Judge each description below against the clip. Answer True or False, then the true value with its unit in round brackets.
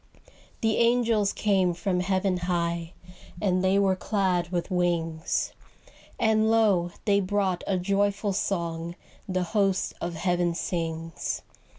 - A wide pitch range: False (2.6 semitones)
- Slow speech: True (120 wpm)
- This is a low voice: False (185 Hz)